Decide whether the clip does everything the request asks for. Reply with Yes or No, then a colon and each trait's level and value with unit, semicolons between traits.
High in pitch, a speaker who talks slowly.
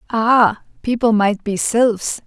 Yes: high, 220 Hz; slow, 130 wpm